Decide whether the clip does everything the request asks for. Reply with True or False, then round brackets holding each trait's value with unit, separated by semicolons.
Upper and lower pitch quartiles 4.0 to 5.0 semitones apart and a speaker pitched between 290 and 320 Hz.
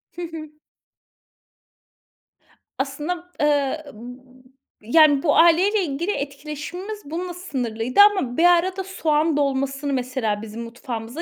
True (4.6 semitones; 295 Hz)